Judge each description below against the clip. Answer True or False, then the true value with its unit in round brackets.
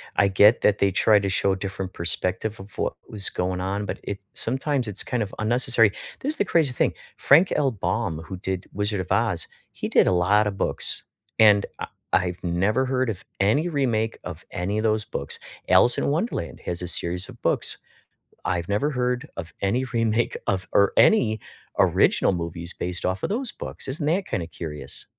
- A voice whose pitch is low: True (105 Hz)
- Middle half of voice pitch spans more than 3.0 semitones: True (5.0 semitones)